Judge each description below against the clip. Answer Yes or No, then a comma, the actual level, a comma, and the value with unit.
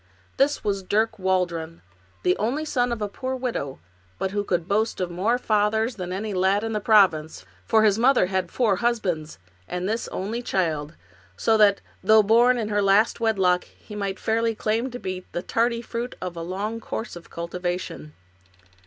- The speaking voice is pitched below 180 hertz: No, high, 205 Hz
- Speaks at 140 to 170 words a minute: No, average, 185 wpm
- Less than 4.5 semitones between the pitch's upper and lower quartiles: Yes, average, 3.8 semitones